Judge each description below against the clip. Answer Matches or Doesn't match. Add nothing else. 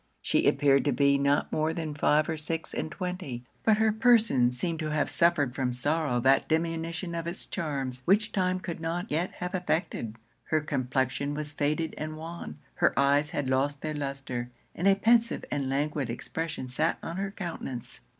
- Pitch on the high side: Doesn't match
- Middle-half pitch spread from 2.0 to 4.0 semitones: Matches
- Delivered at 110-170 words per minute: Doesn't match